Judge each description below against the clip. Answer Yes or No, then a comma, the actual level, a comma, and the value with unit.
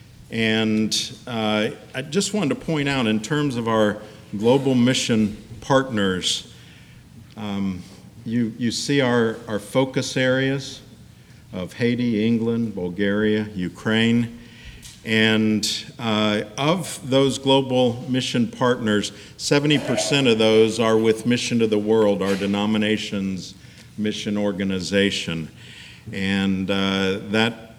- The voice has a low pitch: Yes, low, 110 Hz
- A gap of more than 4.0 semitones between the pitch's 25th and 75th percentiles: No, average, 3.1 semitones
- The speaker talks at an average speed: No, slow, 110 wpm